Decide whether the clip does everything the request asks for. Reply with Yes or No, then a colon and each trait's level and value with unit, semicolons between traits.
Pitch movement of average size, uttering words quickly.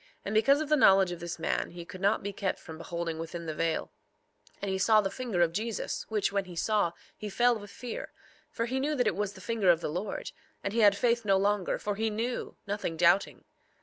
Yes: average, 4.1 semitones; fast, 245 wpm